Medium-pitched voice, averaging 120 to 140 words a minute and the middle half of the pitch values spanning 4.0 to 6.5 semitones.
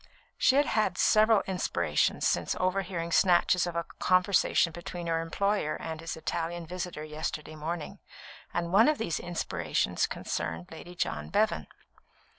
No: medium, 175 Hz; slow, 135 wpm; average, 2.9 semitones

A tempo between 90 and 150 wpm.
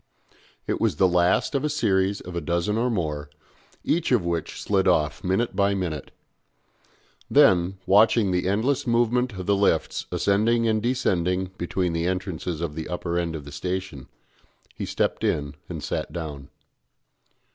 No: average, 165 wpm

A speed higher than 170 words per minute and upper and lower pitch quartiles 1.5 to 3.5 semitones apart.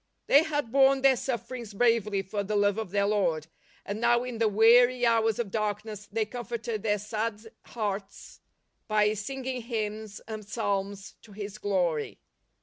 No: average, 155 wpm; average, 2.7 semitones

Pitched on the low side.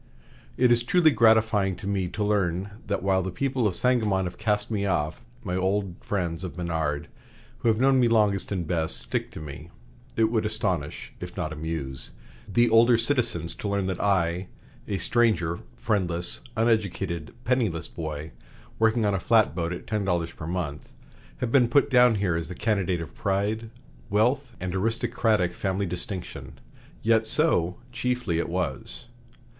Yes: very low, 95 Hz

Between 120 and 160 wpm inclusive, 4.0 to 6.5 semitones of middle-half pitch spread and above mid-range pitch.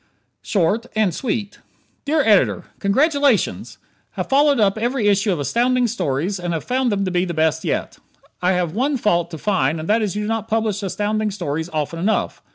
No: average, 180 wpm; average, 4.6 semitones; high, 205 Hz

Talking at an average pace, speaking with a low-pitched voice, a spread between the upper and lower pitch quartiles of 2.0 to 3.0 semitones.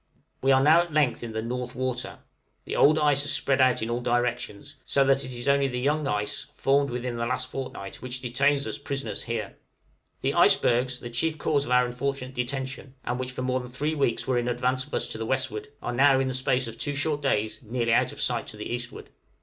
No: fast, 235 wpm; low, 130 Hz; narrow, 2.4 semitones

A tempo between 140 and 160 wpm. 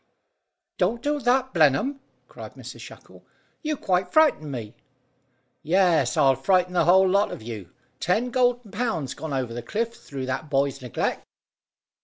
Yes: average, 150 wpm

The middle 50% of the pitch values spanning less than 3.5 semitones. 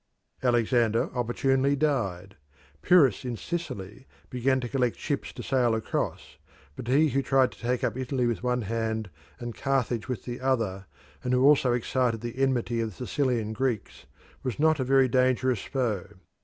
Yes: narrow, 2.6 semitones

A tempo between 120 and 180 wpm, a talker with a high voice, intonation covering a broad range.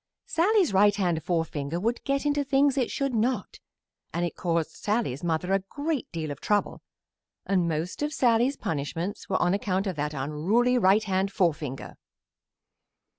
Yes: average, 160 wpm; high, 195 Hz; wide, 7.0 semitones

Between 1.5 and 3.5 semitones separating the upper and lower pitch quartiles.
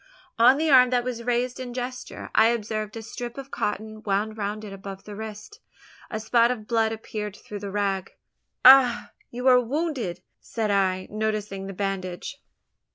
Yes: average, 3.2 semitones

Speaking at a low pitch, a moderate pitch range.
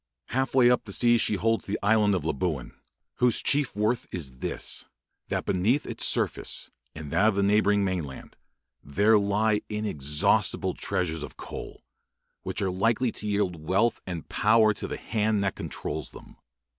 Yes: low, 105 Hz; average, 3.6 semitones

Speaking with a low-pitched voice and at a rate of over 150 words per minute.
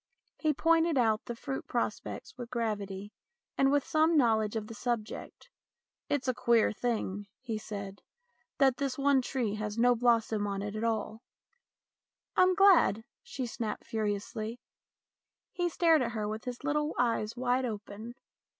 No: high, 235 Hz; average, 170 wpm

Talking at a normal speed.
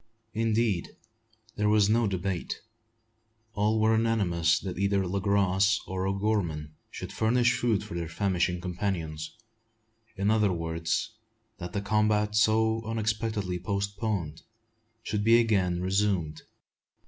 No: slow, 120 wpm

